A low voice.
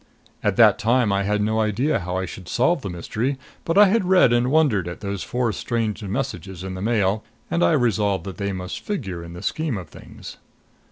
Yes: low, 105 Hz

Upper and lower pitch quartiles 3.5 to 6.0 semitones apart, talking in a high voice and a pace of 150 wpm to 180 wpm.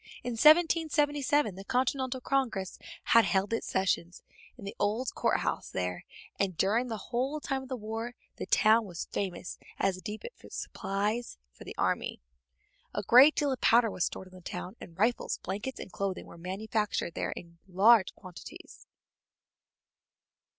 Yes: average, 5.1 semitones; high, 215 Hz; average, 165 wpm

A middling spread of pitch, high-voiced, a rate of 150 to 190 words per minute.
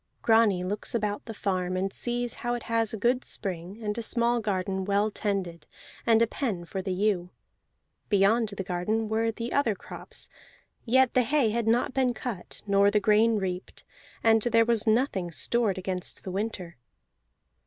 Yes: average, 3.3 semitones; high, 215 Hz; average, 175 wpm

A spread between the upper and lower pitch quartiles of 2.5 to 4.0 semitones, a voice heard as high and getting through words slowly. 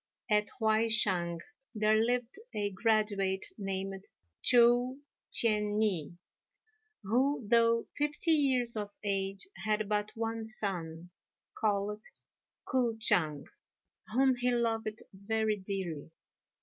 Yes: average, 2.9 semitones; high, 215 Hz; slow, 105 wpm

